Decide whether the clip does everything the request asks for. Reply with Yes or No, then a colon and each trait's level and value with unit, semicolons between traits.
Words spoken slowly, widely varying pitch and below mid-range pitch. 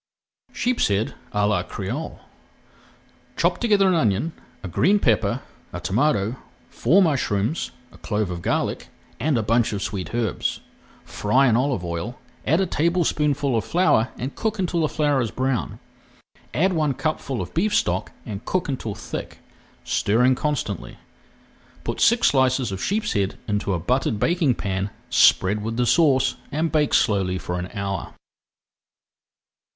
No: average, 145 wpm; wide, 7.3 semitones; low, 125 Hz